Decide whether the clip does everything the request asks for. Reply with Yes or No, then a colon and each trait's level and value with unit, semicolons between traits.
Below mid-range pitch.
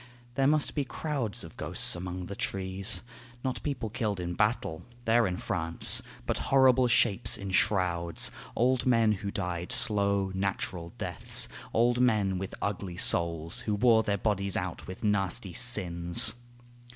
Yes: low, 100 Hz